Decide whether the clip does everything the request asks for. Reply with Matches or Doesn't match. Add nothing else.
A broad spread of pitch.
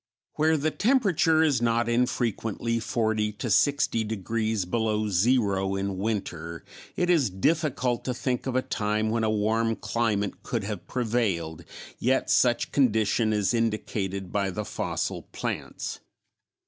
Doesn't match